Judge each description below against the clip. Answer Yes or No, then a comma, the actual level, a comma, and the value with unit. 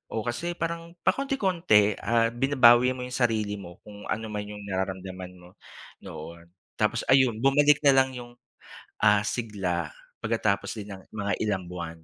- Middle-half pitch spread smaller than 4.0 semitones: No, average, 5.1 semitones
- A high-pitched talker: No, low, 110 Hz